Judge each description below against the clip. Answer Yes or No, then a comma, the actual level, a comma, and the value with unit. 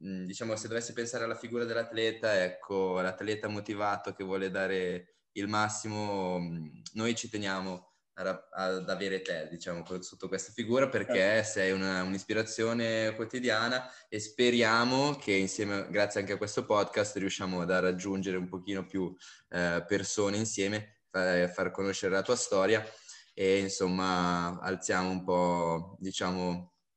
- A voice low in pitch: Yes, very low, 95 Hz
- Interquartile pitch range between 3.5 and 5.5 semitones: No, average, 2.8 semitones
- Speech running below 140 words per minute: Yes, average, 130 wpm